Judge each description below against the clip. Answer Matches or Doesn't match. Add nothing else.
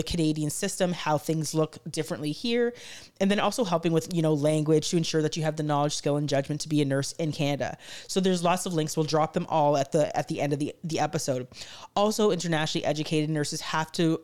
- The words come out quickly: Matches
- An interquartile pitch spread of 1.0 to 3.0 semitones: Matches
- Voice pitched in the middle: Matches